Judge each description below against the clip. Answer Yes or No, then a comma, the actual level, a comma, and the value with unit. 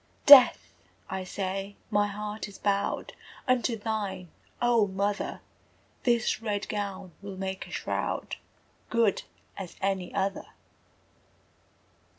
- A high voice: Yes, high, 200 Hz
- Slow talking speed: Yes, slow, 110 wpm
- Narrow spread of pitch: Yes, narrow, 2.1 semitones